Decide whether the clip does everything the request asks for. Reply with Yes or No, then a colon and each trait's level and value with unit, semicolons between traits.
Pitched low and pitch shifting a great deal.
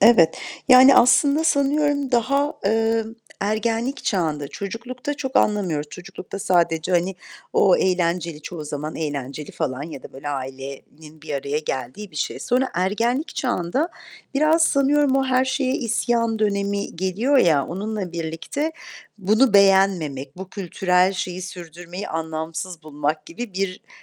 No: high, 190 Hz; wide, 7.3 semitones